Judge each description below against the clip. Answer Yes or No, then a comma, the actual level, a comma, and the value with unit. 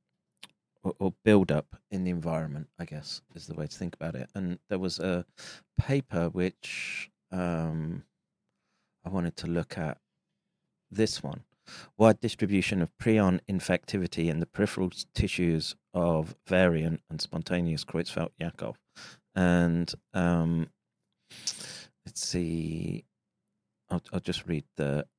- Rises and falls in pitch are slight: Yes, narrow, 2.3 semitones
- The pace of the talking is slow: Yes, slow, 125 wpm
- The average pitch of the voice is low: Yes, very low, 90 Hz